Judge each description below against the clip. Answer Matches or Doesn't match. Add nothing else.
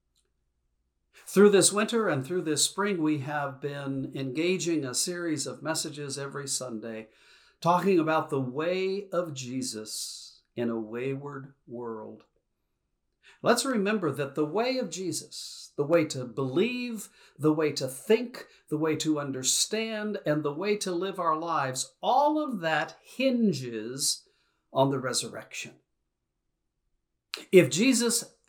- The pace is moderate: Doesn't match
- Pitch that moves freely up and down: Matches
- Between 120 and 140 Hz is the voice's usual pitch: Doesn't match